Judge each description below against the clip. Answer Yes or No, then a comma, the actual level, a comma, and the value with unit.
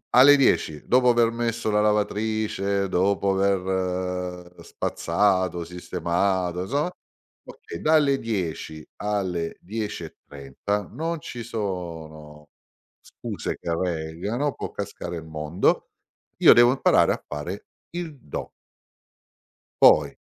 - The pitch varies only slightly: No, average, 4.7 semitones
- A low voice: Yes, very low, 95 Hz